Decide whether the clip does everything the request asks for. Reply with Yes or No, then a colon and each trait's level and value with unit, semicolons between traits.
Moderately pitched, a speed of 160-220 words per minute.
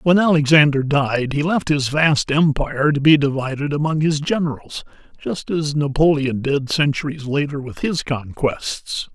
No: medium, 145 Hz; average, 150 wpm